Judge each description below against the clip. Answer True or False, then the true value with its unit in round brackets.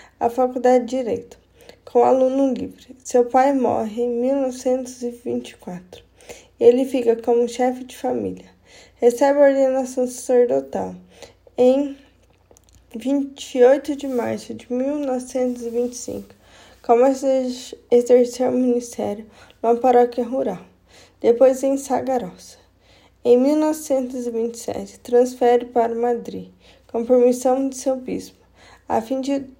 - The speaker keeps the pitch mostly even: True (1.8 semitones)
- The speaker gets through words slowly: True (105 wpm)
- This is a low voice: False (250 Hz)